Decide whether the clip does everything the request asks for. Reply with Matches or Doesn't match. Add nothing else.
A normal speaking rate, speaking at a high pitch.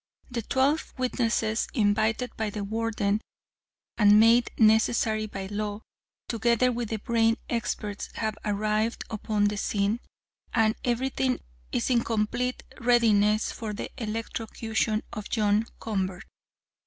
Doesn't match